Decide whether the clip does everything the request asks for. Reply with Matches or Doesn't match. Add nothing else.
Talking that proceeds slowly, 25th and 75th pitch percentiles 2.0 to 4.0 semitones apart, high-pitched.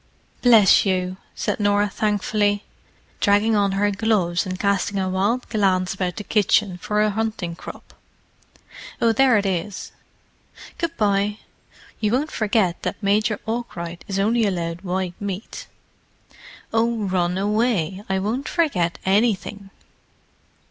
Matches